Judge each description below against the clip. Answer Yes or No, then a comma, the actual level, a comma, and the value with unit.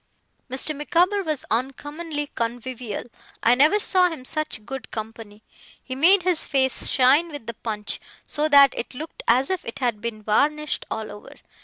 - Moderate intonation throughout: Yes, average, 4.9 semitones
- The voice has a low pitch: No, very high, 270 Hz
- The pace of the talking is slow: No, average, 165 wpm